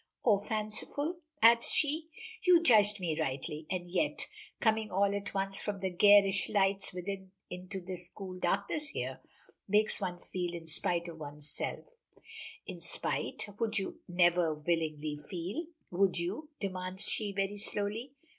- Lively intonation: No, average, 3.2 semitones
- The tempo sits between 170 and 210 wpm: No, average, 145 wpm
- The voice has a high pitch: Yes, high, 195 Hz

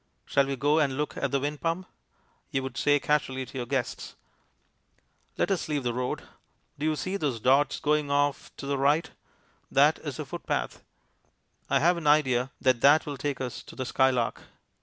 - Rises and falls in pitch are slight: Yes, narrow, 2.2 semitones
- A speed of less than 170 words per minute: No, average, 190 wpm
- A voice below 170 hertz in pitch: Yes, medium, 140 Hz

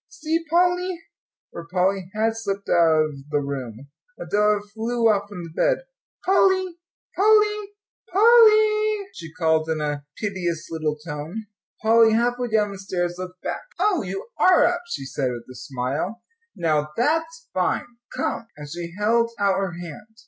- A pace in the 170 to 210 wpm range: No, average, 160 wpm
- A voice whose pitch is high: Yes, high, 200 Hz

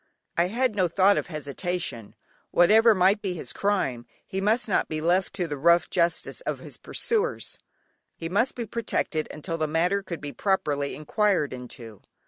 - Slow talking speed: No, average, 170 wpm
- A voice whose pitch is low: No, medium, 175 Hz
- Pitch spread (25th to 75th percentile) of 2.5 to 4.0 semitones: No, average, 4.8 semitones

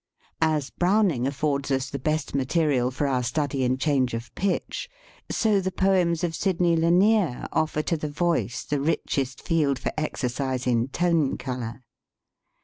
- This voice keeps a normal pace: Yes, average, 155 wpm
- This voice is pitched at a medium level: Yes, medium, 145 Hz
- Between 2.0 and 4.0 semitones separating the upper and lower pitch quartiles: No, average, 4.5 semitones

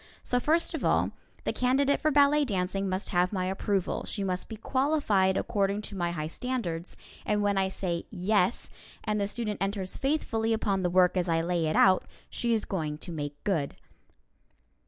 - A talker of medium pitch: No, high, 195 Hz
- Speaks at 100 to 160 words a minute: No, average, 185 wpm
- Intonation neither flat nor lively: Yes, average, 3.9 semitones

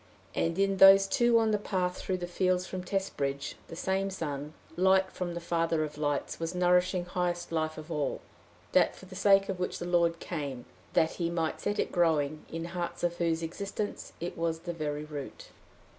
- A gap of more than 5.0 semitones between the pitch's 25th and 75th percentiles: No, narrow, 2.6 semitones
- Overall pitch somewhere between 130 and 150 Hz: No, medium, 175 Hz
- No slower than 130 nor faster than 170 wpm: No, average, 195 wpm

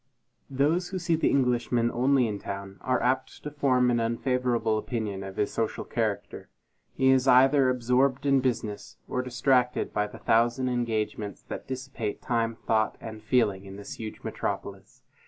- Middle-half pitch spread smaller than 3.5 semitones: Yes, average, 3.0 semitones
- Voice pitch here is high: No, low, 125 Hz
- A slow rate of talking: No, average, 160 wpm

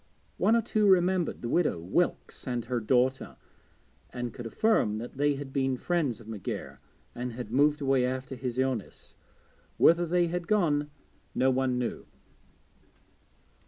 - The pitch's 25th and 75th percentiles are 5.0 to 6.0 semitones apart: Yes, wide, 5.6 semitones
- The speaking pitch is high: No, low, 130 Hz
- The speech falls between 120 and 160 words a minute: Yes, average, 150 wpm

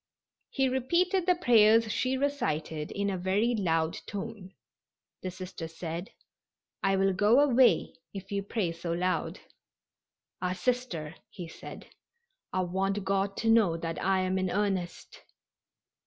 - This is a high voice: Yes, high, 195 Hz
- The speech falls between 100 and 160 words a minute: Yes, average, 140 wpm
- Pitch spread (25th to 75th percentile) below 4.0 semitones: No, average, 4.4 semitones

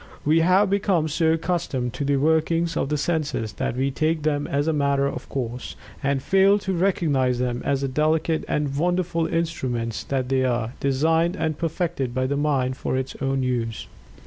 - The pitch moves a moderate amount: Yes, average, 3.9 semitones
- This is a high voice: No, medium, 145 Hz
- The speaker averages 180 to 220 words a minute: Yes, average, 185 wpm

